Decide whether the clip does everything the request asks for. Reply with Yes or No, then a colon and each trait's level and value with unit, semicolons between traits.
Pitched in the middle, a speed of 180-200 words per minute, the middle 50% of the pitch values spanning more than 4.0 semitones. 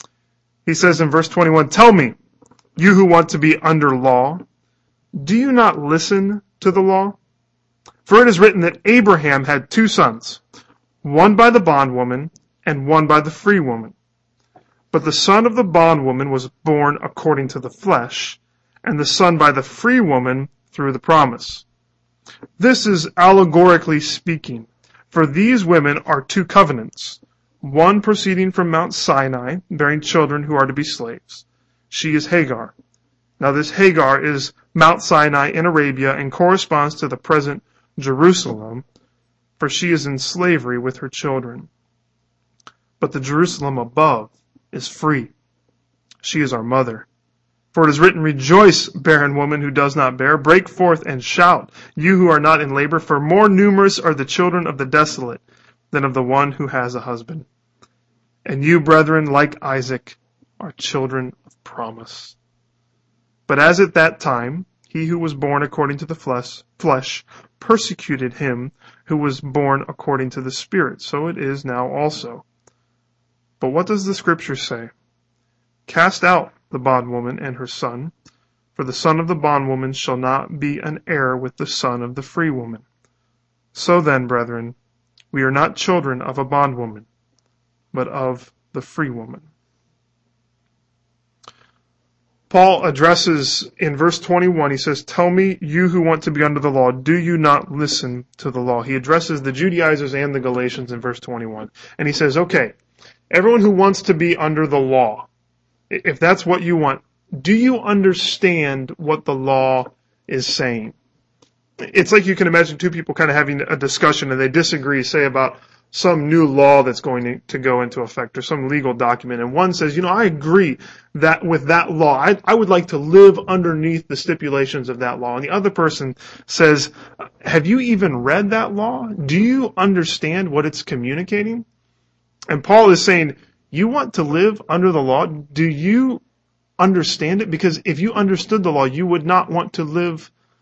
No: medium, 150 Hz; average, 170 wpm; average, 5.2 semitones